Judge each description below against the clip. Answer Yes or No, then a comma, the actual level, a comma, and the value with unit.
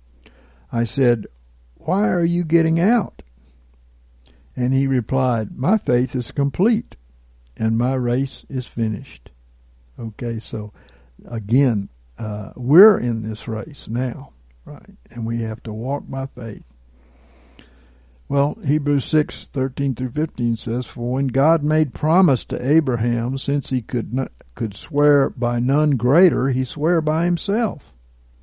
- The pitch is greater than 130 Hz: No, low, 120 Hz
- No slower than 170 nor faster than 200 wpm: No, slow, 135 wpm